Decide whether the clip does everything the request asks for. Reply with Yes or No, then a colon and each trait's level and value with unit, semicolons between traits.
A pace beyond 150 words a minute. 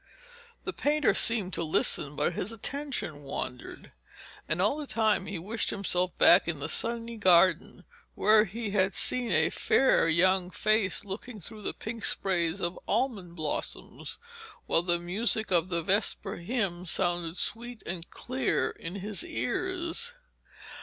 No: average, 145 wpm